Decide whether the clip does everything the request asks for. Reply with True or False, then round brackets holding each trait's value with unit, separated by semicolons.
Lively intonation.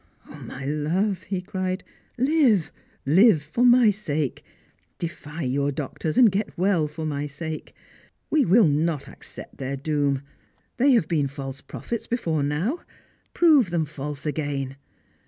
True (6.1 semitones)